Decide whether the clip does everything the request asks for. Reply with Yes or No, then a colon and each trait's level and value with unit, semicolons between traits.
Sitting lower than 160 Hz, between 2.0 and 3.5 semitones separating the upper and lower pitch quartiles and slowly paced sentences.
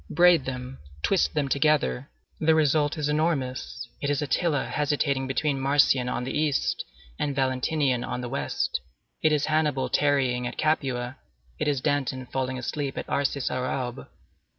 No: medium, 140 Hz; narrow, 2.6 semitones; average, 155 wpm